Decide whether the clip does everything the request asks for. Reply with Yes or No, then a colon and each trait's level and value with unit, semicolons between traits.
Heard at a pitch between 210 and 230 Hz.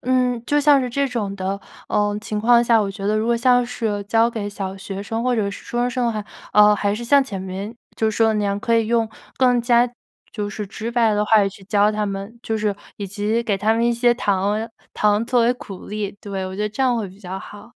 Yes: high, 215 Hz